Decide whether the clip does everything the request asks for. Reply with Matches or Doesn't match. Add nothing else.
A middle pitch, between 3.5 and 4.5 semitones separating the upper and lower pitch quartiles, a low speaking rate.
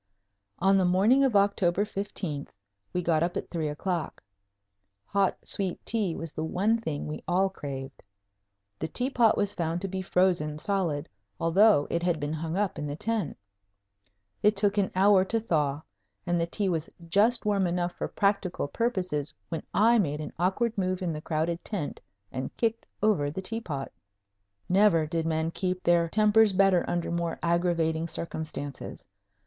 Doesn't match